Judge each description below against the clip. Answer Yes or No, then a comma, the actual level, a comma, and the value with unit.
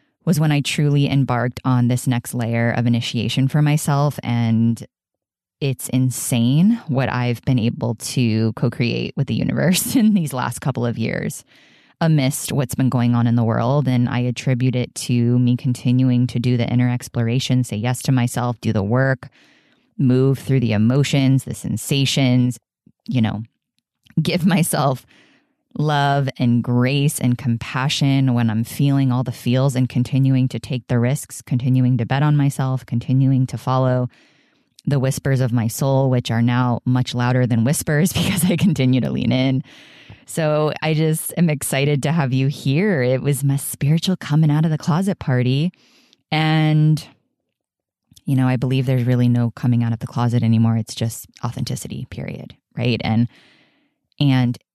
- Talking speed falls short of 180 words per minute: Yes, average, 165 wpm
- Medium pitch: No, low, 130 Hz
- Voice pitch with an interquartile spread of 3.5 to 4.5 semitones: No, average, 3.0 semitones